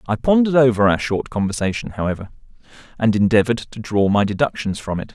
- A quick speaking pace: No, average, 175 wpm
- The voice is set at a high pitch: No, low, 110 Hz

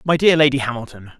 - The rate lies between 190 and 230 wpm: Yes, average, 200 wpm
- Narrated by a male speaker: Yes, male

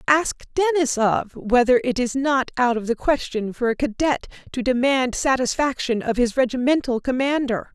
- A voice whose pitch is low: No, very high, 255 Hz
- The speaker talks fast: No, average, 155 wpm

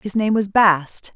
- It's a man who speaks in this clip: No, female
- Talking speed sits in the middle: No, fast, 210 wpm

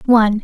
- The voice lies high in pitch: Yes, high, 225 Hz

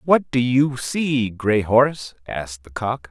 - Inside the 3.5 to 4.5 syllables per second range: Yes, 3.8 syllables/s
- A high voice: No, low, 120 Hz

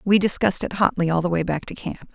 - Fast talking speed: Yes, fast, 280 wpm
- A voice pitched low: No, medium, 185 Hz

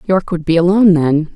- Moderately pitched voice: Yes, medium, 170 Hz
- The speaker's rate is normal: No, fast, 220 wpm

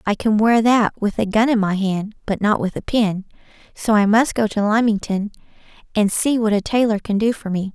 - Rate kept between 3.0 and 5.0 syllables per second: No, 5.2 syllables/s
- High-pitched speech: Yes, high, 215 Hz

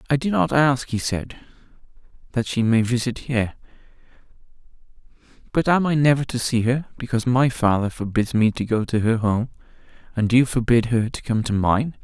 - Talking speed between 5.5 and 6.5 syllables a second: No, 5.3 syllables/s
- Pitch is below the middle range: Yes, low, 120 Hz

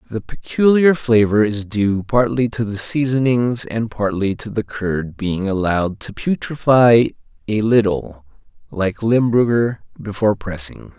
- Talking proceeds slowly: Yes, slow, 130 wpm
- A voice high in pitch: No, low, 110 Hz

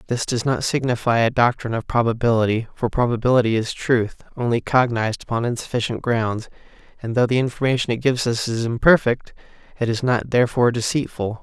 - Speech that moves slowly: No, average, 165 wpm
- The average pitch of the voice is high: No, low, 120 Hz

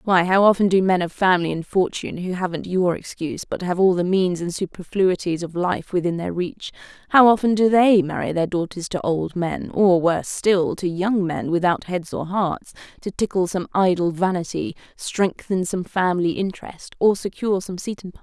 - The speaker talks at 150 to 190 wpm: No, average, 200 wpm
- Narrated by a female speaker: Yes, female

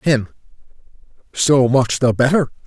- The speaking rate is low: Yes, slow, 115 wpm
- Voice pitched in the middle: No, low, 130 Hz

